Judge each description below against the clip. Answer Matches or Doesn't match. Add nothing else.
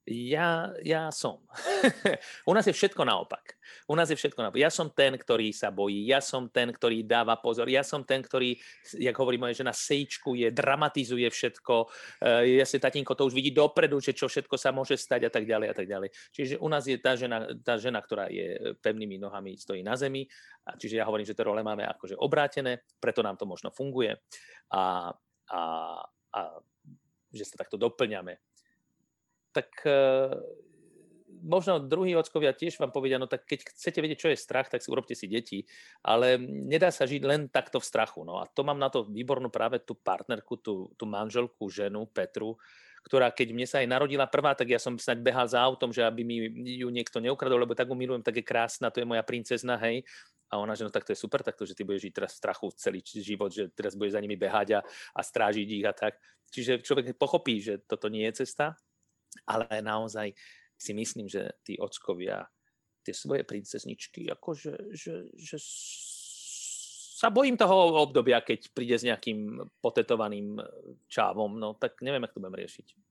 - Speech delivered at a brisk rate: Matches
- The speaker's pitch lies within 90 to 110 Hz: Doesn't match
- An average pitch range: Matches